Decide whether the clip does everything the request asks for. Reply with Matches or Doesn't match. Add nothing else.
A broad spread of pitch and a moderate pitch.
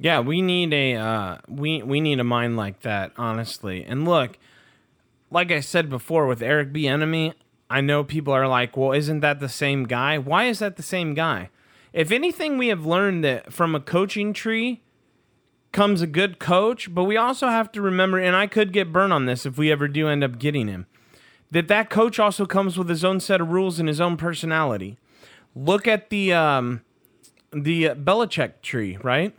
Matches